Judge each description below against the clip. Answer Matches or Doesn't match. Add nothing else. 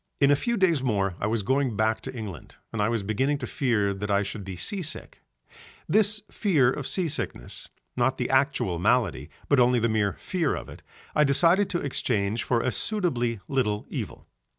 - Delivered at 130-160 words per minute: Doesn't match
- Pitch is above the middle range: Doesn't match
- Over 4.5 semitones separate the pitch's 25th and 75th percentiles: Matches